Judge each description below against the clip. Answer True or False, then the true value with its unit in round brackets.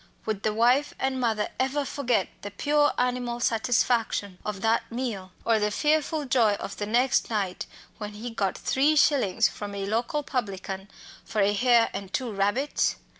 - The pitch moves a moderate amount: True (4.0 semitones)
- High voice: True (230 Hz)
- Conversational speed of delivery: True (170 wpm)